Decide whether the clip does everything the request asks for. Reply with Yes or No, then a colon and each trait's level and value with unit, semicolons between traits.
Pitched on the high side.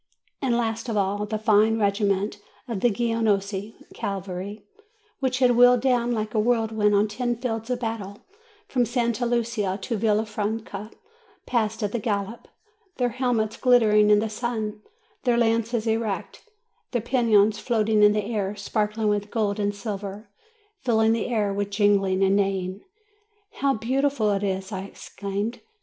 Yes: high, 215 Hz